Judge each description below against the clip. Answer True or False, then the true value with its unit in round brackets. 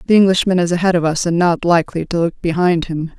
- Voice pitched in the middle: True (175 Hz)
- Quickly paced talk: True (245 wpm)